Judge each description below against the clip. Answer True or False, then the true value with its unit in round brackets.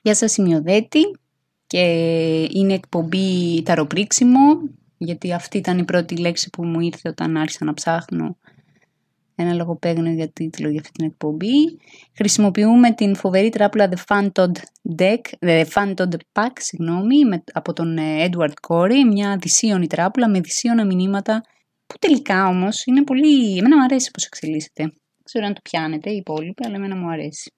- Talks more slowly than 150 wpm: False (155 wpm)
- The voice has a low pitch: False (185 Hz)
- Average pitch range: True (4.4 semitones)